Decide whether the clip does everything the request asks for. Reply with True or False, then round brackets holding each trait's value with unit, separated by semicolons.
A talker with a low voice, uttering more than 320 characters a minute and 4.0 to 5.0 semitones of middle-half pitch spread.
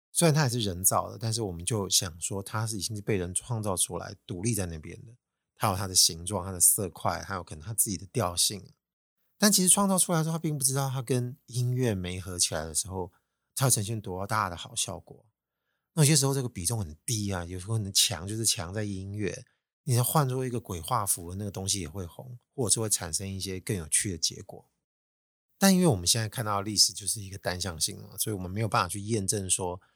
True (105 Hz; 340 characters per minute; 4.5 semitones)